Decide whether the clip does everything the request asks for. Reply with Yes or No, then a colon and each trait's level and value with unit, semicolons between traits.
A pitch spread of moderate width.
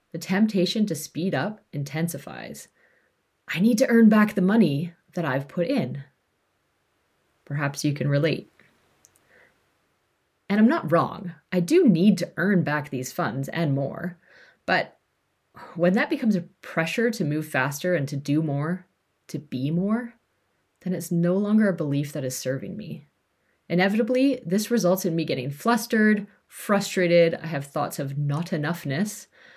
No: wide, 5.7 semitones